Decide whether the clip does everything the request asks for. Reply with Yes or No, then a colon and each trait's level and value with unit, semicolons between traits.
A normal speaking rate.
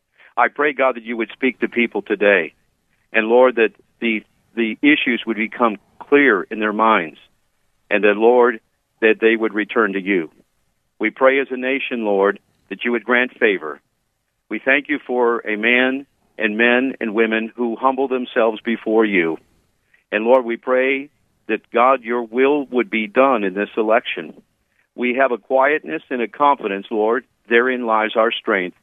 Yes: average, 175 wpm